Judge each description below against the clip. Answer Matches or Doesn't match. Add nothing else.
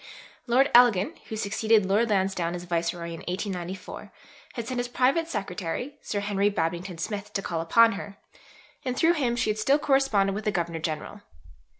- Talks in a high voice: Matches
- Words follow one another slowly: Doesn't match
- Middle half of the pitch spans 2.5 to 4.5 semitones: Doesn't match